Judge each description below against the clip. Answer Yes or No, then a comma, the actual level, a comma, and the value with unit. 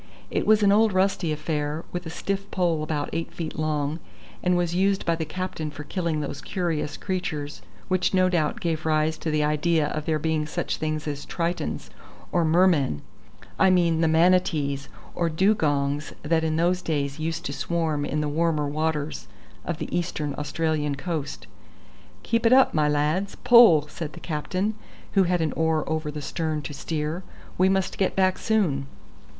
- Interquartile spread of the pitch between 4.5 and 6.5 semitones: No, average, 3.1 semitones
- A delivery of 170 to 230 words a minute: Yes, average, 180 wpm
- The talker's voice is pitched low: No, medium, 160 Hz